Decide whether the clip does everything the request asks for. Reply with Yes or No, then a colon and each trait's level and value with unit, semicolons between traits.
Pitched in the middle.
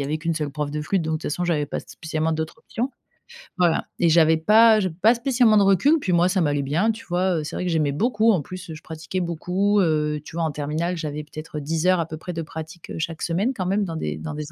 Yes: medium, 165 Hz